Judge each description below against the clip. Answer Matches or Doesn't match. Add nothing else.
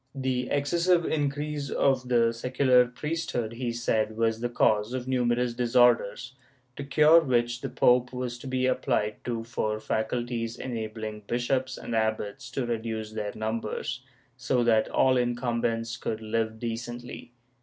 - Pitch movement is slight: Matches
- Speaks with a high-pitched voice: Doesn't match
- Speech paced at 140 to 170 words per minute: Matches